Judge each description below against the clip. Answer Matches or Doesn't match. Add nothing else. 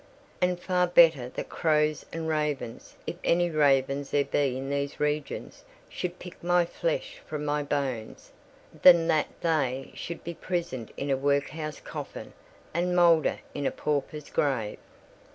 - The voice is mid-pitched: Matches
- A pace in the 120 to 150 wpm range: Matches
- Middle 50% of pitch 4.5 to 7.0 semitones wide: Doesn't match